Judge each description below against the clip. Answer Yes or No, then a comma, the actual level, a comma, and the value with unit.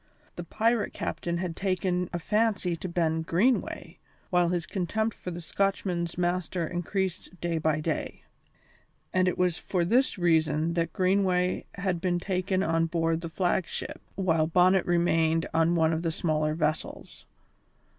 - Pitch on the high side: No, medium, 175 Hz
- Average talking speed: Yes, average, 155 wpm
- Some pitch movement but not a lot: No, narrow, 2.1 semitones